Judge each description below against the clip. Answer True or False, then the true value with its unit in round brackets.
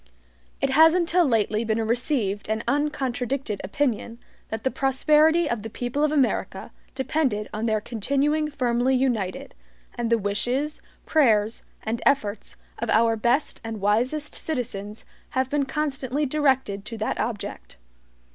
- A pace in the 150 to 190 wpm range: False (140 wpm)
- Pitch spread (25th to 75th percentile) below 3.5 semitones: False (4.7 semitones)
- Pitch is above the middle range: True (245 Hz)